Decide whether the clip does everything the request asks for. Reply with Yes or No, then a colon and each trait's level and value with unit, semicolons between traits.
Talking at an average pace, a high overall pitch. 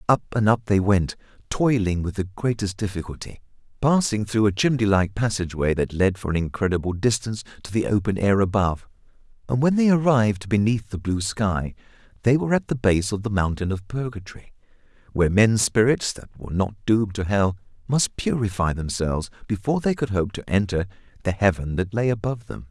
No: average, 180 wpm; low, 105 Hz